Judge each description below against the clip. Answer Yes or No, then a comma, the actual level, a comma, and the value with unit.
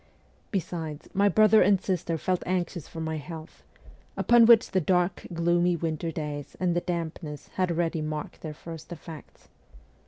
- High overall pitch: No, medium, 170 Hz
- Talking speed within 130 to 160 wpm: Yes, average, 155 wpm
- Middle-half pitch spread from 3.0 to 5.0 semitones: No, narrow, 2.4 semitones